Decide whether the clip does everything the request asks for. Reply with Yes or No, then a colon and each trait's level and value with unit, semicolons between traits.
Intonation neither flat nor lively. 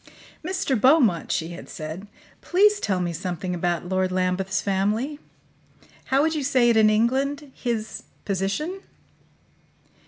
No: wide, 7.2 semitones